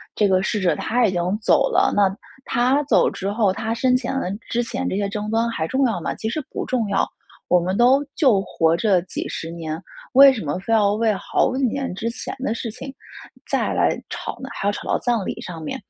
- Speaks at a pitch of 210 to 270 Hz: Yes, high, 215 Hz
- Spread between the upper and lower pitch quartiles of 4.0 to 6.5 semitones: Yes, average, 4.6 semitones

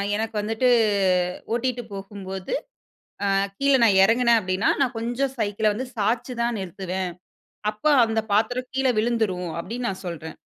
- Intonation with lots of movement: No, average, 3.9 semitones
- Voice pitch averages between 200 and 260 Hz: Yes, high, 220 Hz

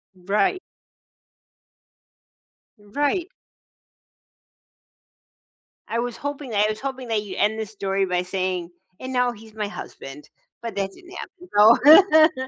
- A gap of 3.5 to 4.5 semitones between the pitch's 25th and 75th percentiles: No, average, 5.2 semitones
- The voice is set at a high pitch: Yes, high, 220 Hz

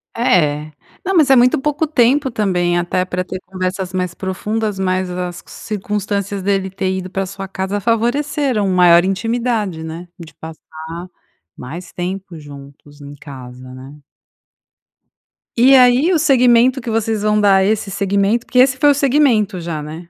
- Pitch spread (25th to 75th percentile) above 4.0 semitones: Yes, average, 5.1 semitones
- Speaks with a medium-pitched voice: No, high, 195 Hz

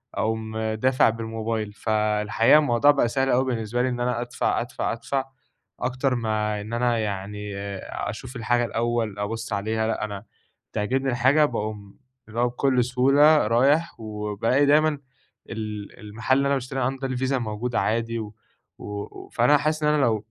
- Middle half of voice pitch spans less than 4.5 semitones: Yes, average, 3.3 semitones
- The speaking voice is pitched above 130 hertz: No, low, 115 Hz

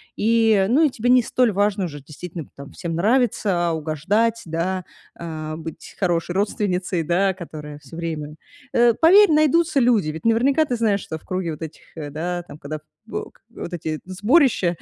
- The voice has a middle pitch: Yes, medium, 180 Hz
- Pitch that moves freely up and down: Yes, wide, 6.2 semitones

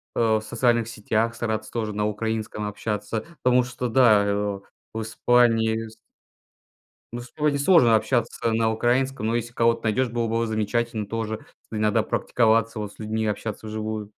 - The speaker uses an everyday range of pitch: No, narrow, 1.7 semitones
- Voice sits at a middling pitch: No, low, 110 Hz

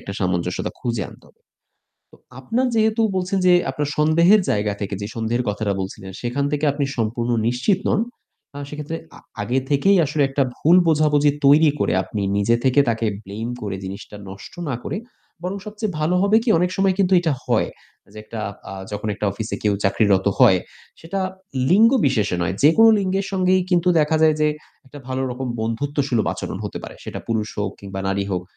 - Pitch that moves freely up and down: Yes, wide, 8.7 semitones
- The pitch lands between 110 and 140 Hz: Yes, low, 135 Hz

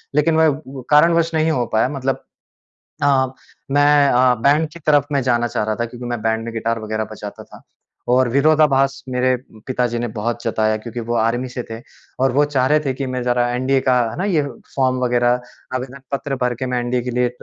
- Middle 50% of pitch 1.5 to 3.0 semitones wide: Yes, average, 2.7 semitones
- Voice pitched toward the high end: No, low, 130 Hz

